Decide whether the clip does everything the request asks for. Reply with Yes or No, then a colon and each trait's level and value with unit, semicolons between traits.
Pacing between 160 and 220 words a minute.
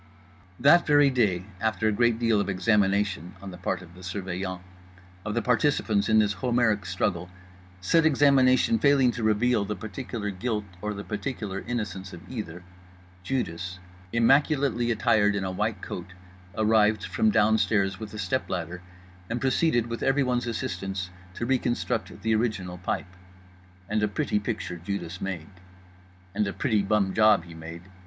No: average, 150 wpm